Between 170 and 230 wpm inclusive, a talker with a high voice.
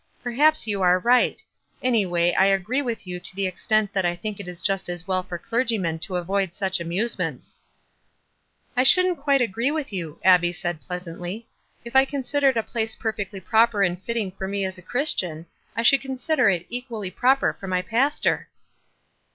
Yes: average, 195 wpm; high, 200 Hz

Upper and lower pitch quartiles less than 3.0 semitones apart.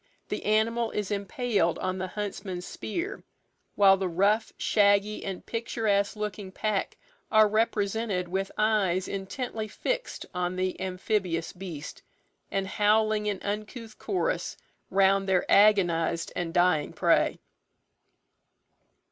Yes: narrow, 2.5 semitones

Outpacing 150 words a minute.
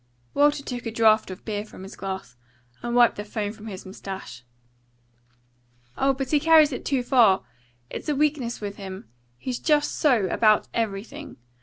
Yes: average, 170 wpm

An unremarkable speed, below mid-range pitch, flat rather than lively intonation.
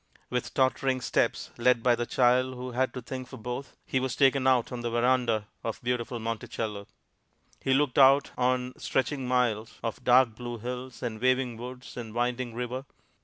Yes: average, 175 wpm; low, 125 Hz; narrow, 1.5 semitones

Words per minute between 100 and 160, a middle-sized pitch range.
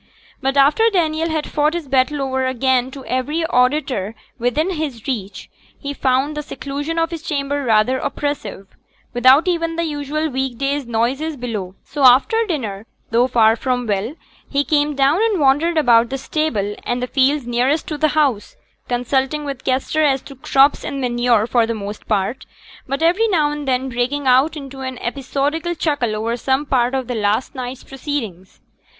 No: average, 175 wpm; average, 3.5 semitones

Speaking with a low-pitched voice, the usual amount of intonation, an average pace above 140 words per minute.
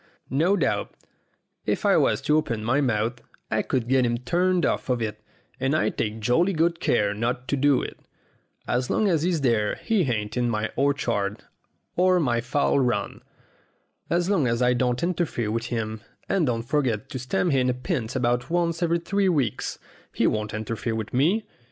No: low, 125 Hz; wide, 6.1 semitones; average, 185 wpm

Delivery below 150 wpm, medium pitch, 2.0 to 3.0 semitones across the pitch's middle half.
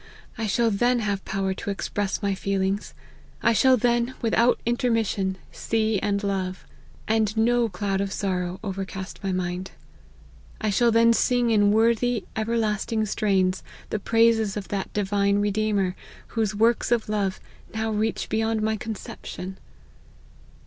No: average, 140 wpm; high, 210 Hz; narrow, 2.6 semitones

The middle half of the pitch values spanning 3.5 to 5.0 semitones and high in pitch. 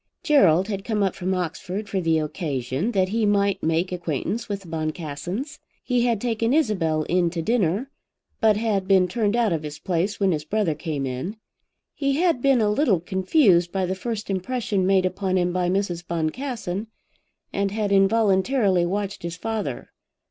Yes: average, 4.0 semitones; high, 195 Hz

